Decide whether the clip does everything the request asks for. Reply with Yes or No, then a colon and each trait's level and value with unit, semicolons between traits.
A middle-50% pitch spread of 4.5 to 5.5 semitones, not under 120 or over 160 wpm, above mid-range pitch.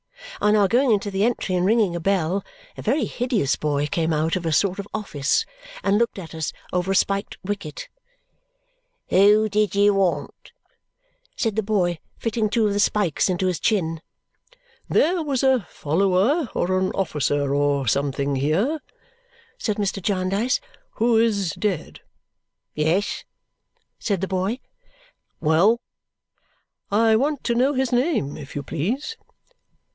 Yes: average, 5.1 semitones; average, 150 wpm; high, 195 Hz